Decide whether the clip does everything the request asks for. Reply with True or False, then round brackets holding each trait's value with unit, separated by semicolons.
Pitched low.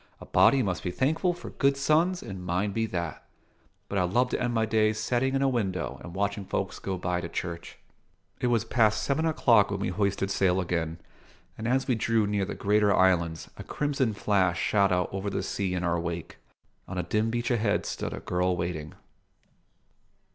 True (100 Hz)